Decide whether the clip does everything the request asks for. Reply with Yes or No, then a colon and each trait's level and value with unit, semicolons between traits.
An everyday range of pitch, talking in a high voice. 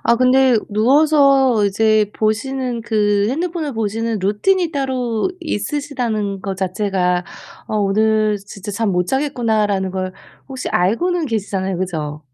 Yes: average, 5.0 semitones; high, 220 Hz